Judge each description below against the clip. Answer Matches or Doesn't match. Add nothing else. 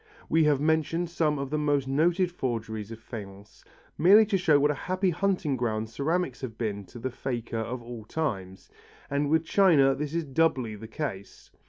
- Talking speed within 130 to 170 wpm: Doesn't match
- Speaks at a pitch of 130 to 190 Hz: Matches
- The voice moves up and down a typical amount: Doesn't match